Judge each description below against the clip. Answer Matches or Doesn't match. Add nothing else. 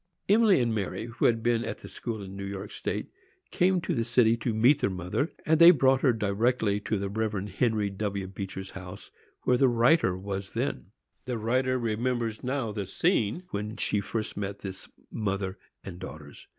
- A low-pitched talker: Matches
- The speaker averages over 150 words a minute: Matches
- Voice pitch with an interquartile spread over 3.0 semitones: Matches